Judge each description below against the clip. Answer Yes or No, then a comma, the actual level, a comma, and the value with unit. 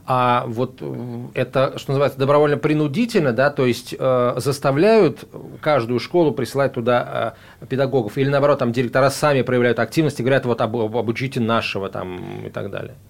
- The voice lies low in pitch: Yes, low, 130 Hz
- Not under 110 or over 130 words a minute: No, fast, 160 wpm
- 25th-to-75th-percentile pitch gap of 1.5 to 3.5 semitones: Yes, average, 2.8 semitones